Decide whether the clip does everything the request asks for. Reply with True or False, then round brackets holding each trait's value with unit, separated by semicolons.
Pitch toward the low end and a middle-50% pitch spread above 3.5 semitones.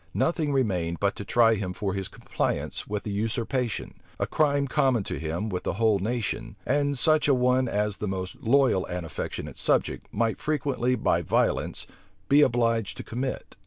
True (115 Hz; 4.8 semitones)